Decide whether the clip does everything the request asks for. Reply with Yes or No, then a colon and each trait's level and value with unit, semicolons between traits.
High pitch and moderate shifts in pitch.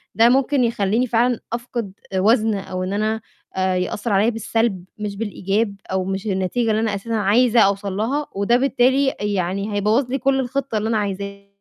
Yes: high, 215 Hz; average, 3.3 semitones